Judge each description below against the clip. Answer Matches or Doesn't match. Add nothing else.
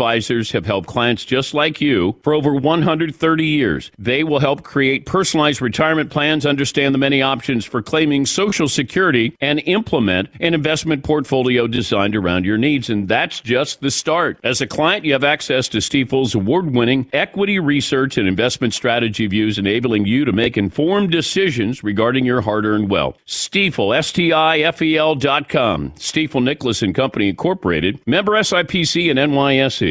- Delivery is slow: Doesn't match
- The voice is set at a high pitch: Doesn't match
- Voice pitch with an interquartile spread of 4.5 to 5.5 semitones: Matches